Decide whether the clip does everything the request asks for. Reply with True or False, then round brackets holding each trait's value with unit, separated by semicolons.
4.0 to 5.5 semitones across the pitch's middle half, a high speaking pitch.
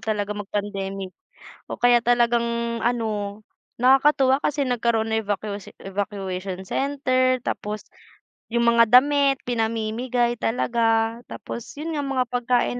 False (3.2 semitones; 235 Hz)